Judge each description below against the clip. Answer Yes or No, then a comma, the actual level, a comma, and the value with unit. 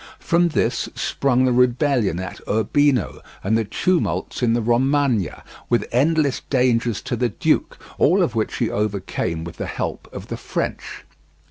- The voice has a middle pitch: No, low, 120 Hz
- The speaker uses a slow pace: No, average, 155 wpm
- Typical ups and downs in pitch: Yes, average, 4.4 semitones